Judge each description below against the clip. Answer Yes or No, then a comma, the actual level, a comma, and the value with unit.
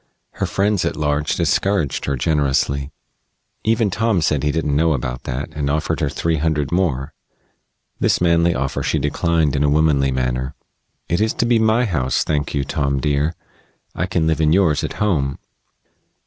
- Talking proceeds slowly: No, average, 175 wpm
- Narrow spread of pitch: No, average, 3.7 semitones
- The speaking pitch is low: Yes, very low, 75 Hz